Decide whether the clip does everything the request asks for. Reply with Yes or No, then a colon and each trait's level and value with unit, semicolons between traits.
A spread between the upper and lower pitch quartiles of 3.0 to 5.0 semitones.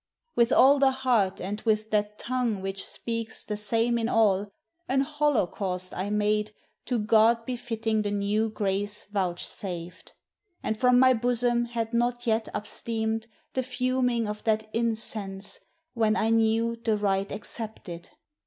No: narrow, 2.4 semitones